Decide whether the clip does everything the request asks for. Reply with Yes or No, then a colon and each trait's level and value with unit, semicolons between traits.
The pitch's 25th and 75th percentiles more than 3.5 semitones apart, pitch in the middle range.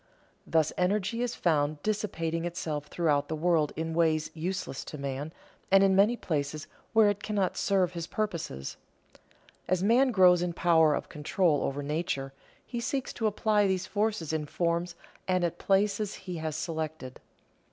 Yes: average, 4.1 semitones; medium, 175 Hz